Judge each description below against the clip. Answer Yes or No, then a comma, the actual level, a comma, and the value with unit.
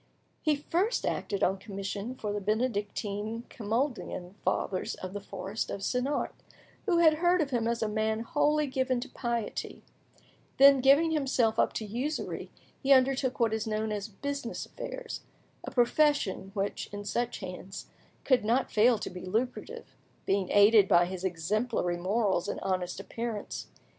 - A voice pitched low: No, high, 225 Hz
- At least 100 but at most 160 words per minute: Yes, average, 155 wpm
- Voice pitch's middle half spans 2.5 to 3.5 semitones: No, average, 4.7 semitones